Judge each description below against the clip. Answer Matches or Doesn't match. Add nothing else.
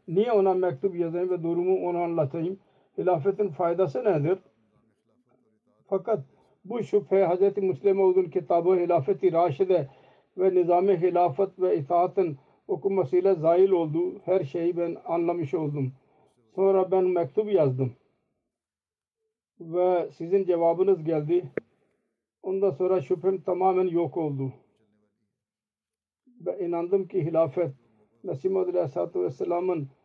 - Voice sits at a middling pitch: Matches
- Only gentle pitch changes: Matches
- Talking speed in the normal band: Matches